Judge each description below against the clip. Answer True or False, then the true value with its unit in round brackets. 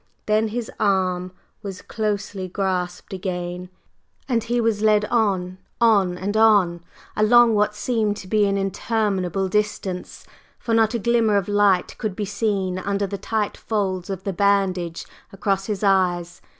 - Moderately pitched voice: False (200 Hz)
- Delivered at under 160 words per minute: True (150 wpm)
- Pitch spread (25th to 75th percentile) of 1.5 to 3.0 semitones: True (2.4 semitones)